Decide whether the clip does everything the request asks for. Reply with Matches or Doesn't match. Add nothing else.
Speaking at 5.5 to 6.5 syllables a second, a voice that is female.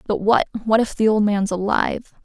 Matches